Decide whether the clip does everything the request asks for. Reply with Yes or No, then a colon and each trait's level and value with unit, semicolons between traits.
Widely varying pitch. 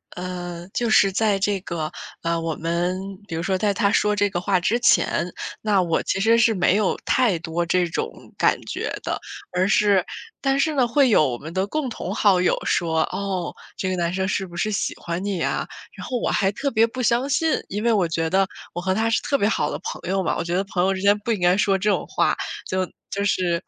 No: average, 3.4 semitones